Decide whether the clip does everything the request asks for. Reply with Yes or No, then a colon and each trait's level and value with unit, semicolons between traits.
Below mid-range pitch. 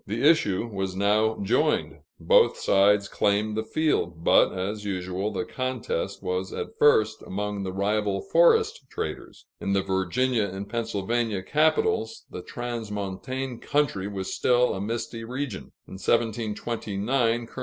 Yes: low, 105 Hz